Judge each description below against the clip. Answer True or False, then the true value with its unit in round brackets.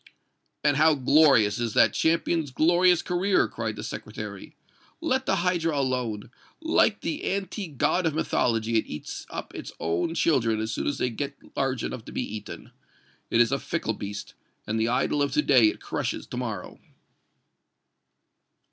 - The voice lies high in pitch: False (140 Hz)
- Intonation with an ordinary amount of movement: False (6.8 semitones)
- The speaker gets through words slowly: False (165 wpm)